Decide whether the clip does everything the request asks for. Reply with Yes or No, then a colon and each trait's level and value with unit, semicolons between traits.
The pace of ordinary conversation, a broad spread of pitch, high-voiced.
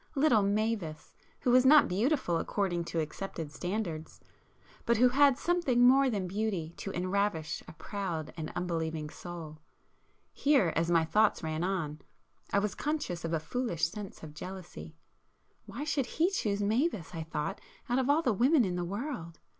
Yes: average, 160 wpm; wide, 6.9 semitones; high, 195 Hz